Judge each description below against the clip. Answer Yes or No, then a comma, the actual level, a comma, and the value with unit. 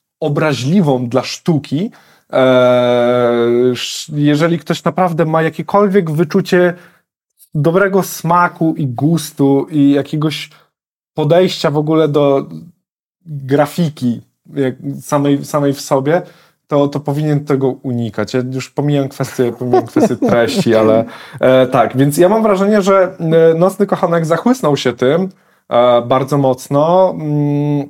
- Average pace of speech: No, slow, 105 wpm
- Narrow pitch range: No, average, 4.2 semitones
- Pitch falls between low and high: Yes, medium, 150 Hz